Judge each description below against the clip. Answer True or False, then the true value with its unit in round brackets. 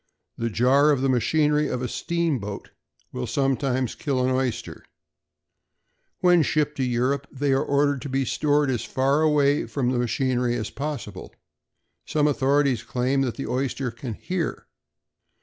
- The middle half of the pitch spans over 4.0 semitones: False (2.7 semitones)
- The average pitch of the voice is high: False (135 Hz)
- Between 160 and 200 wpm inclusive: False (150 wpm)